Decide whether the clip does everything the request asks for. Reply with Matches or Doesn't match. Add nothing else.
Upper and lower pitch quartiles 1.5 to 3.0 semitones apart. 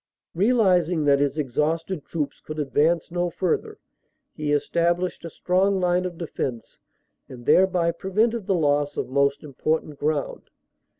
Doesn't match